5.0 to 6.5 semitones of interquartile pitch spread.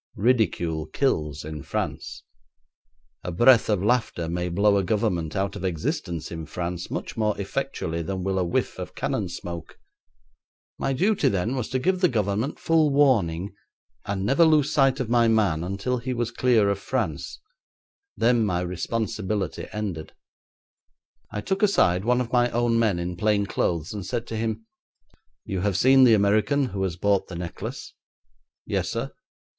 Yes: wide, 5.5 semitones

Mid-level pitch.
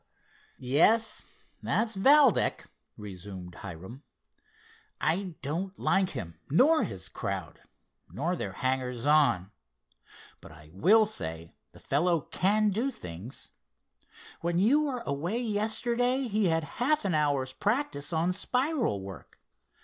Yes: medium, 170 Hz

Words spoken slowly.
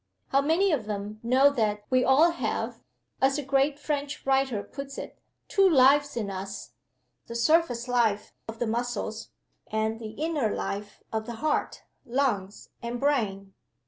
No: average, 155 wpm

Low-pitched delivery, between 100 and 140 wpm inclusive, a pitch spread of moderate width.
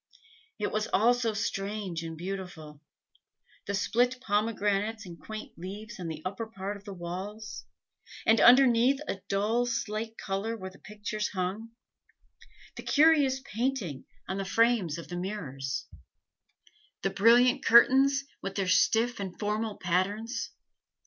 No: high, 210 Hz; slow, 135 wpm; average, 3.3 semitones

